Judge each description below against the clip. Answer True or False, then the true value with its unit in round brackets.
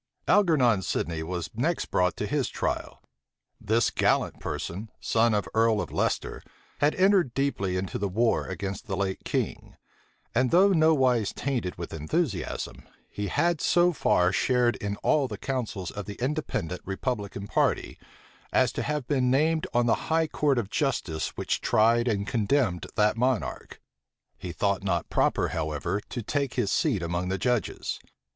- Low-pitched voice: True (115 Hz)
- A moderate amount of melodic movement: False (6.1 semitones)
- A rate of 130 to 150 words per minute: False (160 wpm)